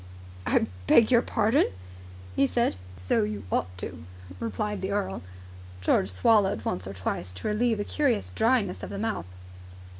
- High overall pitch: Yes, high, 200 Hz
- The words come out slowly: No, average, 155 wpm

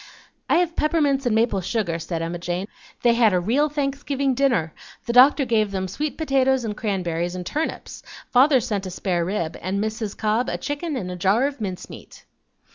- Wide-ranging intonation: Yes, wide, 6.6 semitones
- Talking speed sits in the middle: Yes, average, 195 wpm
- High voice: Yes, high, 220 Hz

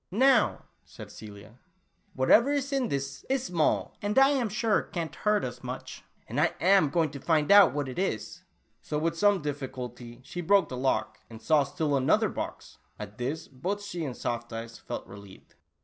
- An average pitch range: No, wide, 8.1 semitones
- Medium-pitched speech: Yes, medium, 155 Hz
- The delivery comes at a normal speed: Yes, average, 195 wpm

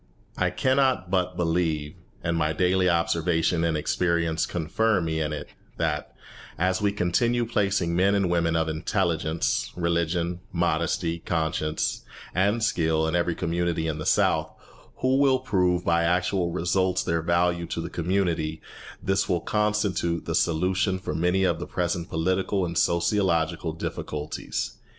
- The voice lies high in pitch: No, very low, 85 Hz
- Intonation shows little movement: Yes, narrow, 2.2 semitones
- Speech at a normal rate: Yes, average, 145 wpm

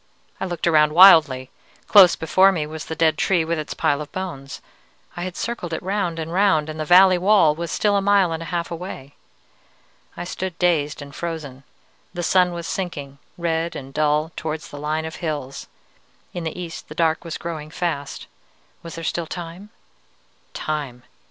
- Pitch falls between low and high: Yes, medium, 165 Hz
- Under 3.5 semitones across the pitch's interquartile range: Yes, average, 2.7 semitones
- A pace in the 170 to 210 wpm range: Yes, average, 185 wpm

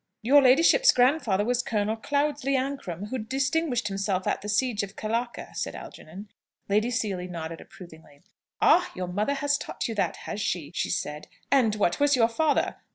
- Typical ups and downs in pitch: No, wide, 5.8 semitones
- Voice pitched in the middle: No, high, 225 Hz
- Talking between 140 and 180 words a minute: Yes, average, 170 wpm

